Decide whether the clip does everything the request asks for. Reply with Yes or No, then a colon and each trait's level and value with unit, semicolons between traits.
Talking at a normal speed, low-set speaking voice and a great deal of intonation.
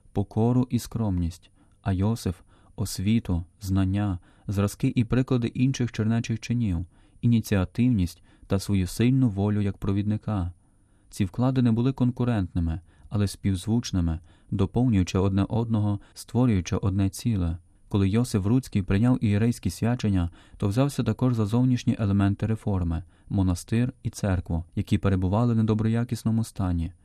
No: average, 120 wpm; low, 105 Hz; average, 3.3 semitones